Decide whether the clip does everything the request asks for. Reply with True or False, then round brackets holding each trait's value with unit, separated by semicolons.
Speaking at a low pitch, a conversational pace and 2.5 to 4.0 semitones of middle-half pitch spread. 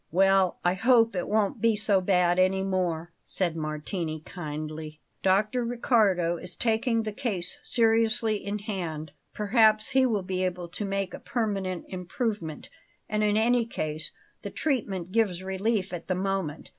False (195 Hz; 155 wpm; 3.7 semitones)